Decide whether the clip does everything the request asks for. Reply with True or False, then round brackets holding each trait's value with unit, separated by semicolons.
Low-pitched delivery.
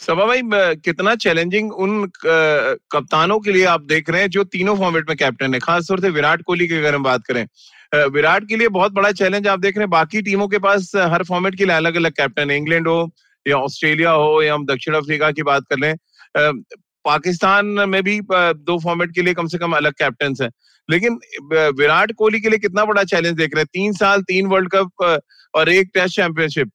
False (175 Hz)